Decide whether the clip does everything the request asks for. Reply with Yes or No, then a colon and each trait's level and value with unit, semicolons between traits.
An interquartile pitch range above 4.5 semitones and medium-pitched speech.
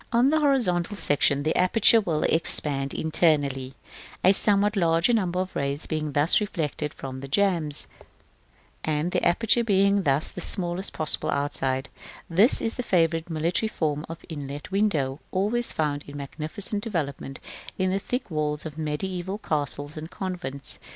Yes: average, 5.1 semitones; medium, 165 Hz